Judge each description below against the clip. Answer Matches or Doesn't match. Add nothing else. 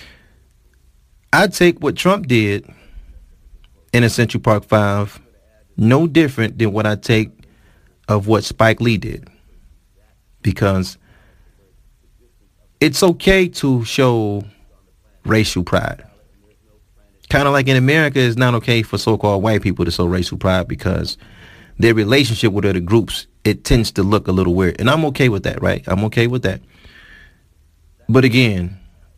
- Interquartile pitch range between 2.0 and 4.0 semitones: Doesn't match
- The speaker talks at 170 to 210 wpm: Doesn't match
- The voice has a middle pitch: Doesn't match